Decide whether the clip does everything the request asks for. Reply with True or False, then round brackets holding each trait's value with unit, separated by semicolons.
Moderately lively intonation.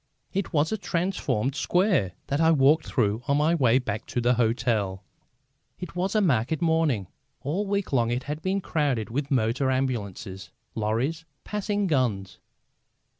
False (6.4 semitones)